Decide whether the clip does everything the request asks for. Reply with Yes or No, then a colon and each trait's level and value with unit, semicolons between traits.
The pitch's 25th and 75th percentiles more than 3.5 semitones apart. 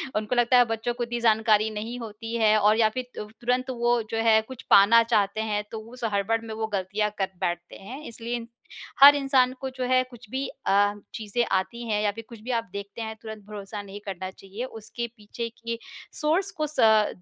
No: narrow, 2.5 semitones